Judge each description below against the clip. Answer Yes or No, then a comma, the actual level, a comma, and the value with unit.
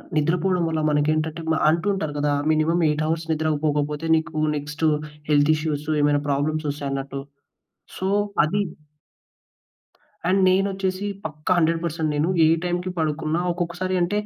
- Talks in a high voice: No, medium, 160 Hz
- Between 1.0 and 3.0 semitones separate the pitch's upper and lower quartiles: Yes, narrow, 2.6 semitones